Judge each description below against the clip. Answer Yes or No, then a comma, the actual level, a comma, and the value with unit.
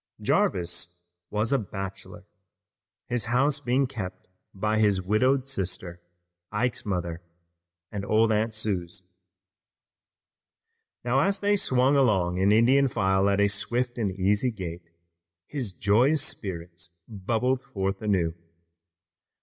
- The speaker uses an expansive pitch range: No, average, 4.9 semitones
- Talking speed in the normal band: No, slow, 115 wpm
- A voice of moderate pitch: No, low, 105 Hz